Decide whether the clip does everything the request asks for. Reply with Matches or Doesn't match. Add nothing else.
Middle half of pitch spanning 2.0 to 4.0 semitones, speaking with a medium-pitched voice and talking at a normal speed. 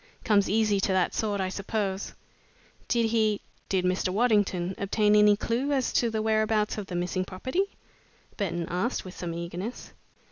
Doesn't match